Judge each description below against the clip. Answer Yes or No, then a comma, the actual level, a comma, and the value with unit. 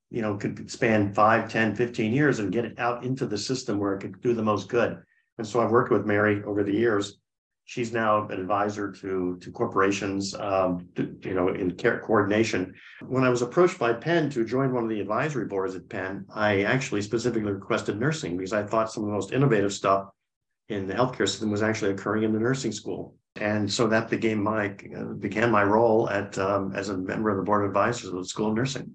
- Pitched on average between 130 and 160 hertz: No, low, 105 Hz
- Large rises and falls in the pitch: No, average, 2.8 semitones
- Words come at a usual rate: No, fast, 225 wpm